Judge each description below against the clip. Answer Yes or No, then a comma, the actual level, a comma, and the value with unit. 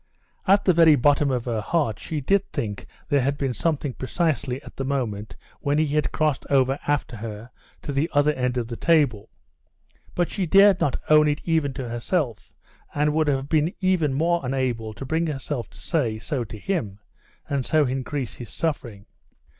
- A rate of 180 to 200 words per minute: Yes, average, 185 wpm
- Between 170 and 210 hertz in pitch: No, medium, 140 Hz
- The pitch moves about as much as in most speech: Yes, average, 4.2 semitones